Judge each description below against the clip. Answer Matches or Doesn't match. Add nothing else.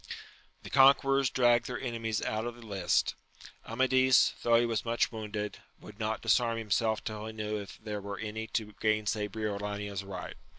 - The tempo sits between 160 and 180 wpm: Matches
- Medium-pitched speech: Doesn't match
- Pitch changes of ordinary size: Doesn't match